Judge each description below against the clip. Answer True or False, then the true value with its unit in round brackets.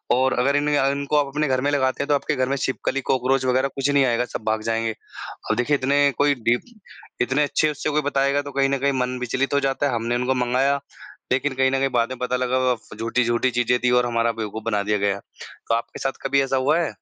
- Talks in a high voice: False (130 Hz)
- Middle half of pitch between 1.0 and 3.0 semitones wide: True (2.4 semitones)